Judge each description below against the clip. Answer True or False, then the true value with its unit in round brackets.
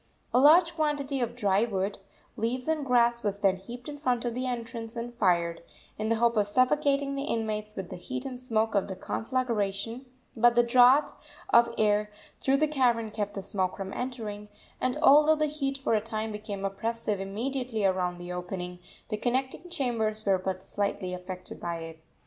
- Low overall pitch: False (230 Hz)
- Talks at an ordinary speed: True (185 wpm)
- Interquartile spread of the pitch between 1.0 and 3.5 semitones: False (4.3 semitones)